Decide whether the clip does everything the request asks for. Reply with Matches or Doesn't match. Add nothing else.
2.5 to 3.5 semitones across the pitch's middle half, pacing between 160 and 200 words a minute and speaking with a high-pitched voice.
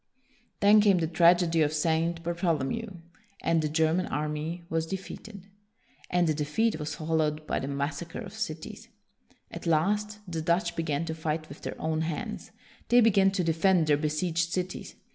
Doesn't match